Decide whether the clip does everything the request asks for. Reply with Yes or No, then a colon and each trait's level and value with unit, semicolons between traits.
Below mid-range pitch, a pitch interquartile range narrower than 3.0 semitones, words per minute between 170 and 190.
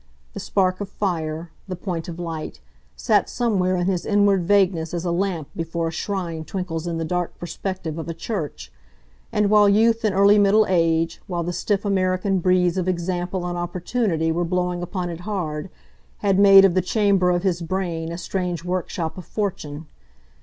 No: medium, 180 Hz; narrow, 2.6 semitones; average, 180 wpm